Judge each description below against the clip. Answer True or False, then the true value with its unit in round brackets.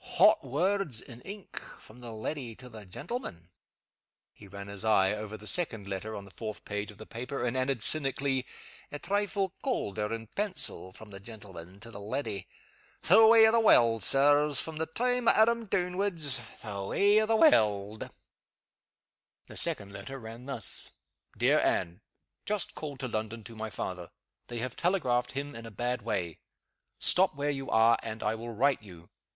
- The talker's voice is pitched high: False (120 Hz)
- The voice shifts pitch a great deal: True (6.7 semitones)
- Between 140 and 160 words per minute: False (180 wpm)